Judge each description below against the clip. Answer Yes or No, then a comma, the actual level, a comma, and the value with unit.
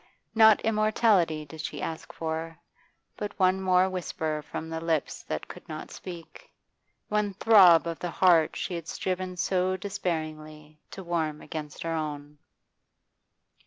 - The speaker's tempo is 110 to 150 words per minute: Yes, average, 140 wpm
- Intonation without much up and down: No, average, 3.0 semitones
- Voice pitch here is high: No, medium, 170 Hz